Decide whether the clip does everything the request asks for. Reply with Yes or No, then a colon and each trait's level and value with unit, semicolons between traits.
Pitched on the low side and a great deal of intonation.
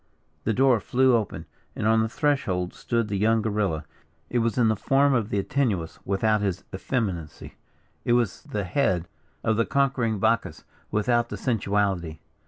No: low, 110 Hz; average, 3.5 semitones